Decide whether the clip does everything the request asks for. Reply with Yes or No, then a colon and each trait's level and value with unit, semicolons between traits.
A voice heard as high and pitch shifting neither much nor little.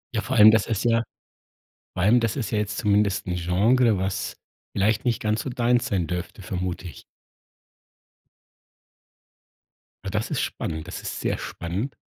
No: low, 105 Hz; average, 3.8 semitones